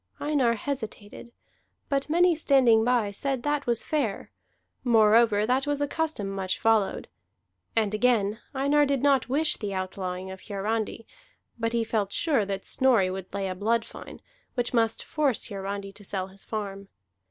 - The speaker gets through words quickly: No, average, 160 wpm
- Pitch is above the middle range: Yes, high, 225 Hz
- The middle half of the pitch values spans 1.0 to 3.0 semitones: No, average, 5.2 semitones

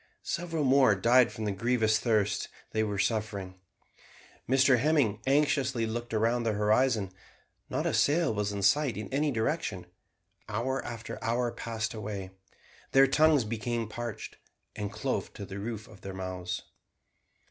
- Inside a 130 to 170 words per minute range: Yes, average, 145 wpm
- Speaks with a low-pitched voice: Yes, low, 115 Hz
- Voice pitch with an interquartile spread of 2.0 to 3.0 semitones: No, average, 3.9 semitones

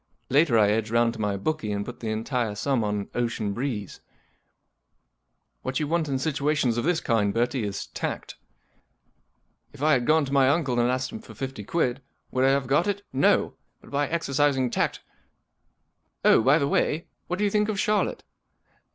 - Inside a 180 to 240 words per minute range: Yes, average, 195 wpm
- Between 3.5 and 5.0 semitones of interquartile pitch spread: Yes, average, 4.6 semitones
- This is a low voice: Yes, low, 130 Hz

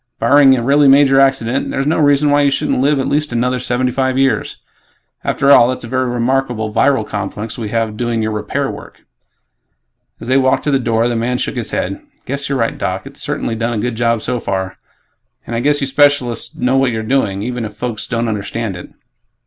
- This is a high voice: No, low, 125 Hz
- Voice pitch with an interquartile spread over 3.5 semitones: No, average, 3.0 semitones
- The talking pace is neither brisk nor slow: No, fast, 215 wpm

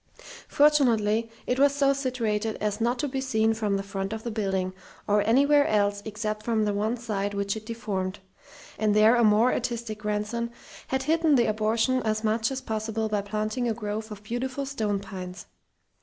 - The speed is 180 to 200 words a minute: Yes, average, 185 wpm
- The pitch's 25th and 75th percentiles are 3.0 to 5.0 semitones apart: No, narrow, 2.6 semitones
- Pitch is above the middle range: Yes, high, 220 Hz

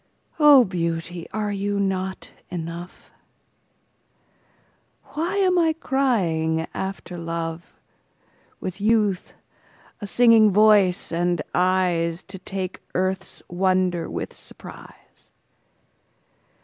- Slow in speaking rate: Yes, slow, 80 wpm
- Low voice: No, medium, 185 Hz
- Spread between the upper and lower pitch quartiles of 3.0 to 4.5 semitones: Yes, average, 3.4 semitones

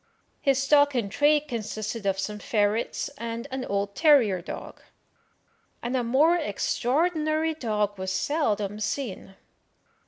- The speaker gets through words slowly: Yes, slow, 125 wpm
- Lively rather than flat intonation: Yes, wide, 6.0 semitones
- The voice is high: Yes, high, 235 Hz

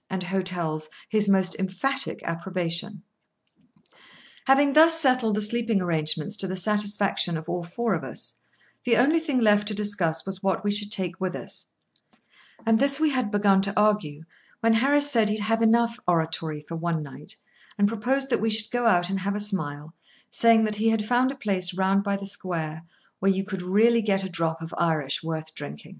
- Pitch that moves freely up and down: No, average, 4.4 semitones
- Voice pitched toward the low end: No, high, 200 Hz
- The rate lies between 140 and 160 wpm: No, average, 190 wpm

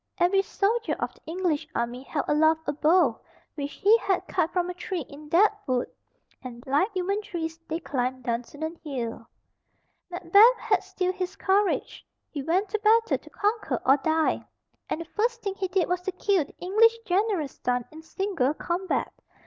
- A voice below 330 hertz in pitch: No, very high, 350 Hz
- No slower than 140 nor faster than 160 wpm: No, average, 175 wpm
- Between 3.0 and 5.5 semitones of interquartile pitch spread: Yes, average, 5.1 semitones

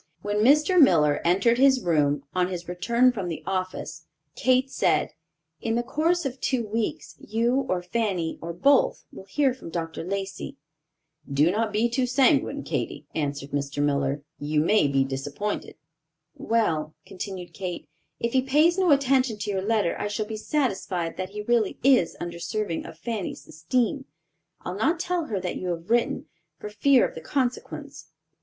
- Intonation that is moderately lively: No, wide, 6.8 semitones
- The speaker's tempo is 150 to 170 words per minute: Yes, average, 165 wpm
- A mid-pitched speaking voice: No, high, 210 Hz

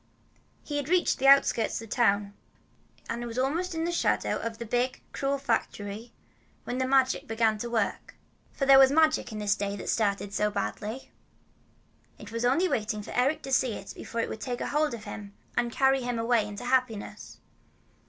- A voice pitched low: No, high, 240 Hz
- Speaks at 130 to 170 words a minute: No, average, 195 wpm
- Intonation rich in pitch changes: No, average, 4.0 semitones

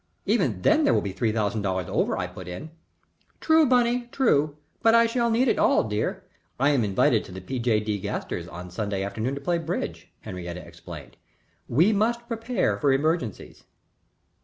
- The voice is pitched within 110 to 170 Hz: Yes, low, 135 Hz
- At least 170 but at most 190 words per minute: Yes, average, 185 wpm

